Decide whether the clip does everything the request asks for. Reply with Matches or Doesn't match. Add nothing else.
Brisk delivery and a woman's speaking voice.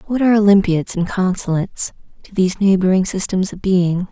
Doesn't match